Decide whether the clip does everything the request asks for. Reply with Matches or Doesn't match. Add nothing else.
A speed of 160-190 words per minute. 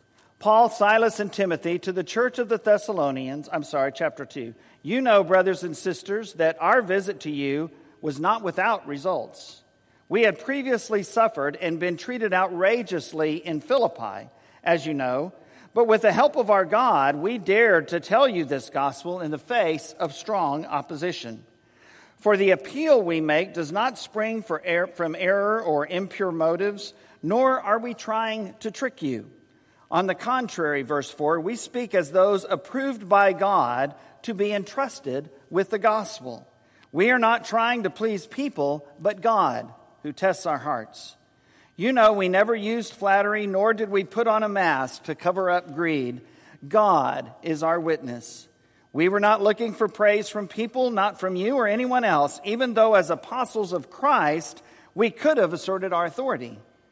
Matches